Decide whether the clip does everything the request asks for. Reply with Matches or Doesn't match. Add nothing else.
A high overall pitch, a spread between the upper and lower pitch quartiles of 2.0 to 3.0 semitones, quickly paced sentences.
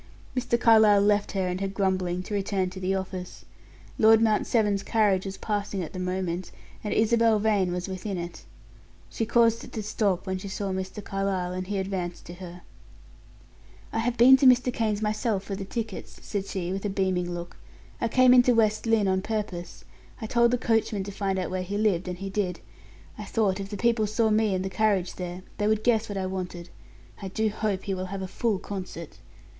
Matches